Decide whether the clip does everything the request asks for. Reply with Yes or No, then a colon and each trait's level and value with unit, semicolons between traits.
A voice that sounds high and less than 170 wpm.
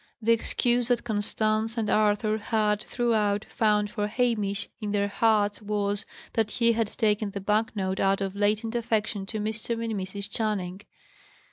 Yes: high, 215 Hz; average, 160 wpm